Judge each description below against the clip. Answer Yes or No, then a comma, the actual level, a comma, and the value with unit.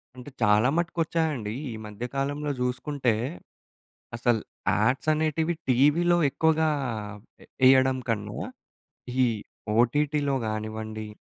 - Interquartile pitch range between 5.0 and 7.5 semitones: Yes, average, 5.3 semitones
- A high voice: No, low, 130 Hz